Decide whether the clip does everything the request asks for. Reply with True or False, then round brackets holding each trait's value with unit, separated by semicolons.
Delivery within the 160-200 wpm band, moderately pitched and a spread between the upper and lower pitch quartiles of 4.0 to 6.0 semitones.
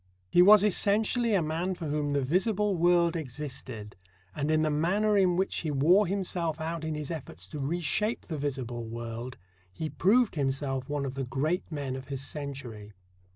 True (180 wpm; 155 Hz; 4.9 semitones)